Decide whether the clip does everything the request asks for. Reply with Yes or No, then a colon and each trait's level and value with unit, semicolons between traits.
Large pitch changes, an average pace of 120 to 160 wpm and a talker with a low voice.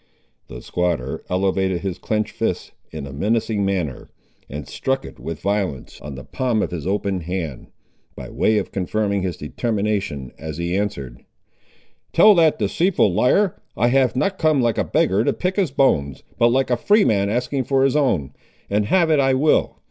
No: wide, 7.0 semitones; average, 180 wpm; low, 105 Hz